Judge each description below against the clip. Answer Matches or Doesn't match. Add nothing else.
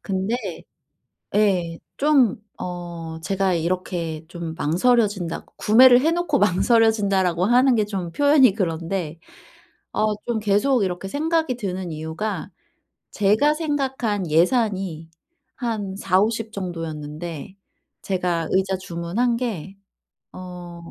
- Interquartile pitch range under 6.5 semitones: Matches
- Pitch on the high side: Matches